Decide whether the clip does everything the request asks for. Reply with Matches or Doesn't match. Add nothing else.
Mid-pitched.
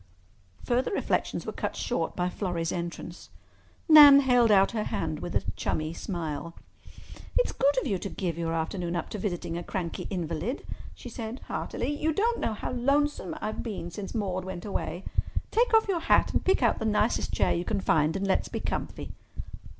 Doesn't match